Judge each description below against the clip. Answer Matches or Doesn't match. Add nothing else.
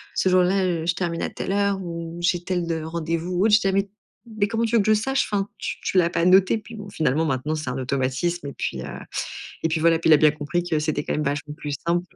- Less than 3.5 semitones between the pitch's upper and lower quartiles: Doesn't match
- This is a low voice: Doesn't match